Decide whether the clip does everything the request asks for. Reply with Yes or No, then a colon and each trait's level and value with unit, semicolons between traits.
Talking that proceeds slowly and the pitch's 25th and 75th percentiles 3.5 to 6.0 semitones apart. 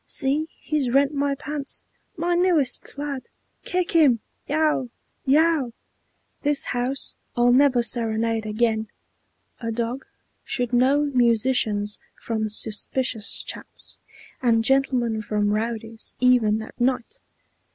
Yes: slow, 110 wpm; average, 3.9 semitones